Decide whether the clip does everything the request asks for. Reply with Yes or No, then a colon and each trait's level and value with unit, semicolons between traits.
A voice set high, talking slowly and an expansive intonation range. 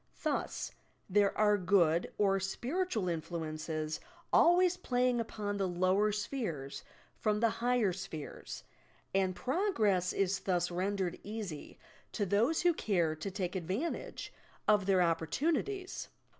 No: high, 200 Hz; slow, 120 wpm; average, 4.6 semitones